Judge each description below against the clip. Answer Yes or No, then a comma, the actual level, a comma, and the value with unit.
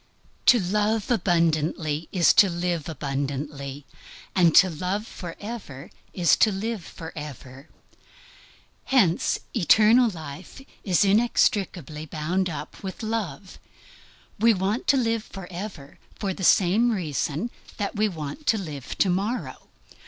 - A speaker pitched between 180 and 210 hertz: Yes, medium, 185 Hz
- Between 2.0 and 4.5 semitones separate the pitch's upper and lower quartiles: No, average, 5.3 semitones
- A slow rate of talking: Yes, slow, 120 wpm